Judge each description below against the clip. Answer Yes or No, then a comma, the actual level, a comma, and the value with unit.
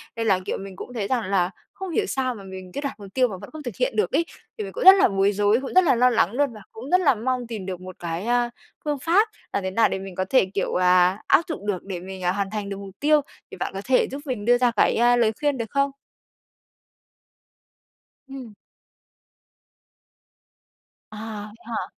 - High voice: Yes, high, 230 Hz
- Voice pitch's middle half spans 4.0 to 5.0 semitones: No, wide, 5.6 semitones